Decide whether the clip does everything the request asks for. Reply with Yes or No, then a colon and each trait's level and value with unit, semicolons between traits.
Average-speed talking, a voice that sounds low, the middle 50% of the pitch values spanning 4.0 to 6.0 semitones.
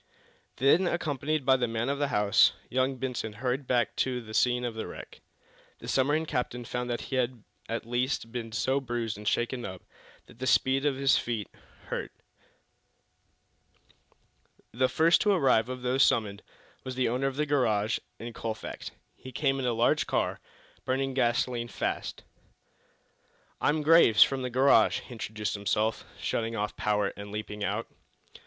No: average, 160 wpm; low, 125 Hz; average, 3.0 semitones